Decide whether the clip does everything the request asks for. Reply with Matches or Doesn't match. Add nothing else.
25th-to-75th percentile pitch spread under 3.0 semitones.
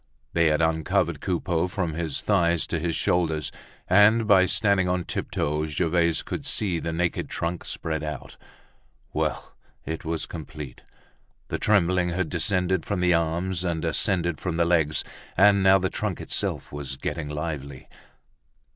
Matches